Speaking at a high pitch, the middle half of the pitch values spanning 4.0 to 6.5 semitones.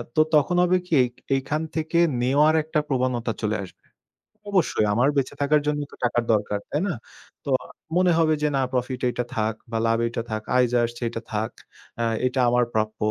No: low, 125 Hz; average, 4.7 semitones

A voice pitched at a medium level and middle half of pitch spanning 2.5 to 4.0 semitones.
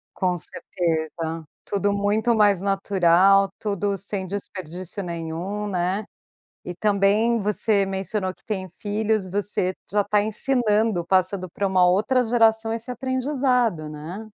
No: high, 200 Hz; average, 2.8 semitones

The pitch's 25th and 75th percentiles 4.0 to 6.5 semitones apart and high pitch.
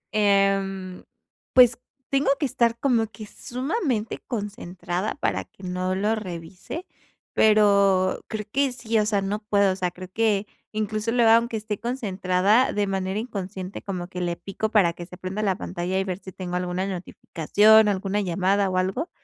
No: average, 2.9 semitones; high, 200 Hz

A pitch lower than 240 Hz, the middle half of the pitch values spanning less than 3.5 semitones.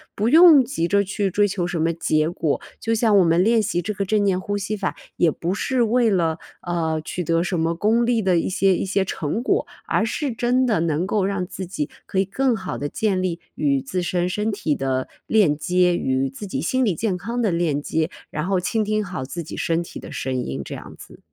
No: medium, 185 Hz; average, 4.3 semitones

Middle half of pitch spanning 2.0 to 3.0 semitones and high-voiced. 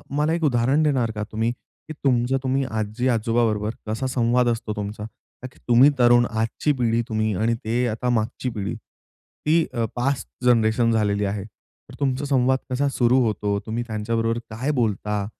No: average, 2.7 semitones; low, 115 Hz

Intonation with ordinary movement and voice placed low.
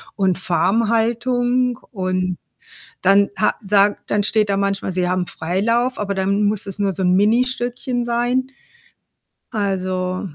No: average, 3.9 semitones; high, 205 Hz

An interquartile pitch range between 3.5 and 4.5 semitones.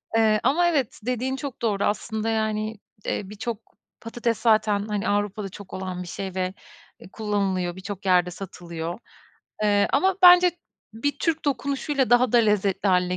Yes: average, 3.9 semitones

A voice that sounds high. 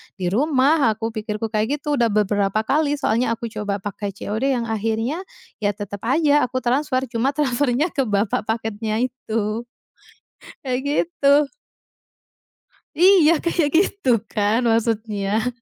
Yes: high, 230 Hz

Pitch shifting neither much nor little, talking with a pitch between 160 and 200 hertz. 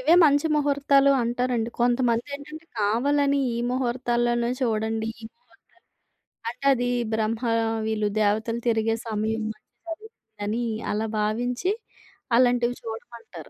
No: average, 3.7 semitones; high, 240 Hz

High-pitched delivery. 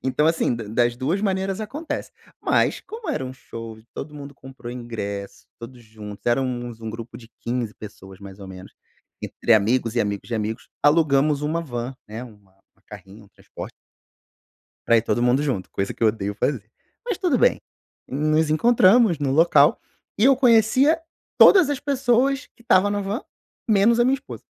No: low, 130 Hz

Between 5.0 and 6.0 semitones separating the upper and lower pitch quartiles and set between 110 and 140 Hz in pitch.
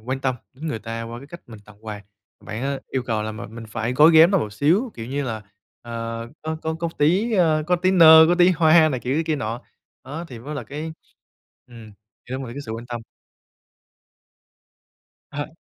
Yes: wide, 5.6 semitones; low, 135 Hz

